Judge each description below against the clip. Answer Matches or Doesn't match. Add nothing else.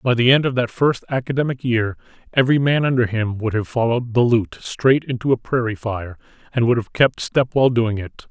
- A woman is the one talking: Doesn't match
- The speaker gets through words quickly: Matches